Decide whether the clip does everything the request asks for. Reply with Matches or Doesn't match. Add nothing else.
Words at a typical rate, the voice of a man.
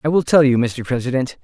Doesn't match